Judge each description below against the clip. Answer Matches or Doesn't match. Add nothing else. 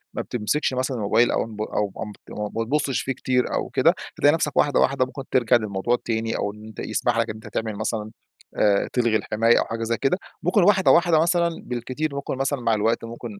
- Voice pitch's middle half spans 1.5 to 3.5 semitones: Doesn't match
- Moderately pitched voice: Doesn't match